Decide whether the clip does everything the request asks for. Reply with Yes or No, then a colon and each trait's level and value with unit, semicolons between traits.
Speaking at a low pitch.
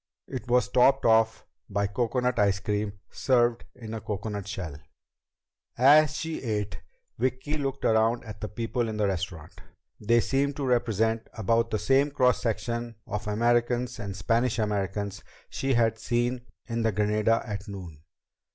Yes: low, 115 Hz